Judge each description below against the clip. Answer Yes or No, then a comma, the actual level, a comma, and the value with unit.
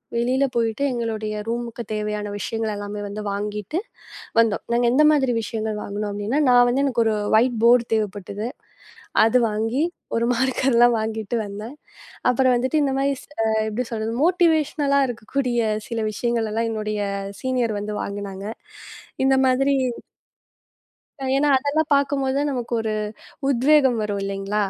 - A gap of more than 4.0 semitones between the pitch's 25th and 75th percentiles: No, average, 3.7 semitones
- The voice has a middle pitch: No, high, 235 Hz